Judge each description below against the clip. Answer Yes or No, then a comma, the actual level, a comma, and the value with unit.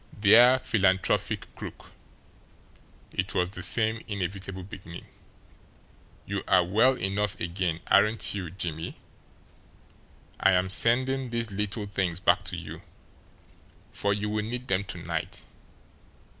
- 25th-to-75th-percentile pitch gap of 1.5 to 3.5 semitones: Yes, average, 3.0 semitones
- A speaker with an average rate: No, slow, 120 wpm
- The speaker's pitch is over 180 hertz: No, low, 100 Hz